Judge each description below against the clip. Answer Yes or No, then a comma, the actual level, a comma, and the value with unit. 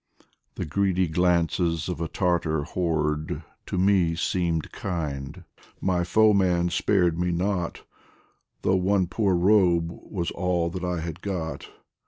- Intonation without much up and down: Yes, narrow, 2.0 semitones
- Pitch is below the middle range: Yes, very low, 90 Hz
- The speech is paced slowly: Yes, slow, 130 wpm